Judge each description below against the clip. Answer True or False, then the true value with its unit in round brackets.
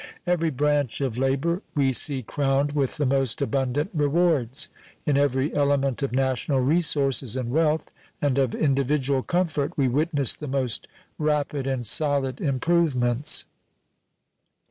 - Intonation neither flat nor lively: False (2.3 semitones)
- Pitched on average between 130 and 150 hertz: True (140 Hz)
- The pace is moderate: False (130 wpm)